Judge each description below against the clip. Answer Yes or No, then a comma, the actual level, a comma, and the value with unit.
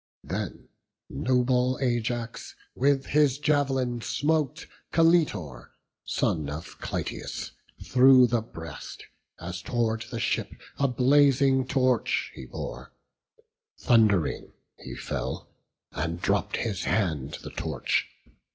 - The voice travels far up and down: Yes, wide, 6.6 semitones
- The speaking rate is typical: No, slow, 105 wpm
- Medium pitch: No, low, 125 Hz